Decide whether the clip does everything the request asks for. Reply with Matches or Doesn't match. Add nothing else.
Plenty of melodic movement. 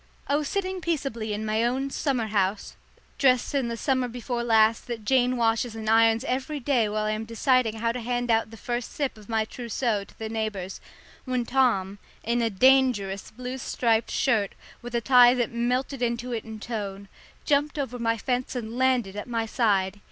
Doesn't match